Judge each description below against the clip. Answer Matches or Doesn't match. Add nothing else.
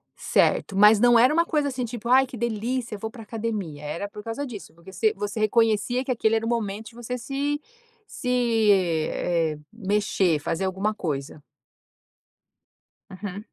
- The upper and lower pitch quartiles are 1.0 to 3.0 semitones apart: Doesn't match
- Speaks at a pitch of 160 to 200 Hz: Doesn't match